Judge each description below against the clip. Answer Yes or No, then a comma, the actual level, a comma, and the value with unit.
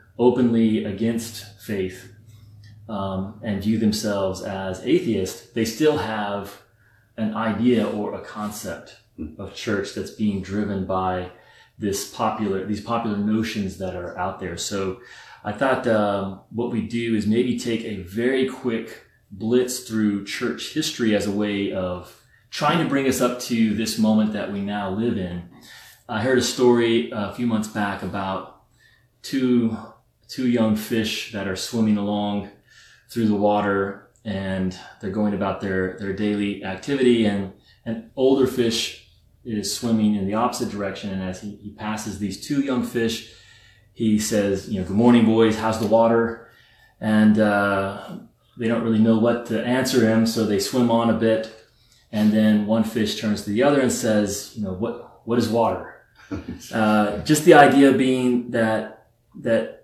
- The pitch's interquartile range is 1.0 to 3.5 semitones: Yes, narrow, 2.4 semitones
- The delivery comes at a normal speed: Yes, average, 160 wpm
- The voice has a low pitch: Yes, low, 110 Hz